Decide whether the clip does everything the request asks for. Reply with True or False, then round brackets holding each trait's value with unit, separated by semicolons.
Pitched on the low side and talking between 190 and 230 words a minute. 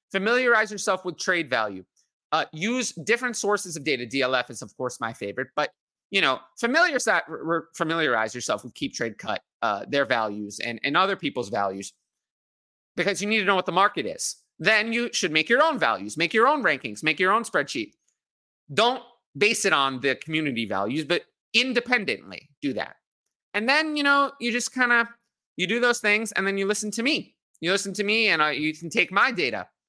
False (195 Hz; 200 wpm)